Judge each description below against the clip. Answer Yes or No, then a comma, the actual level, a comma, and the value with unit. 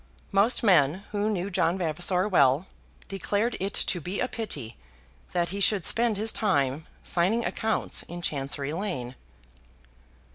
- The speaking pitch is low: No, medium, 185 Hz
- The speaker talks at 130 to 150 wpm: Yes, average, 145 wpm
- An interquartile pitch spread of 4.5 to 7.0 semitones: Yes, average, 4.8 semitones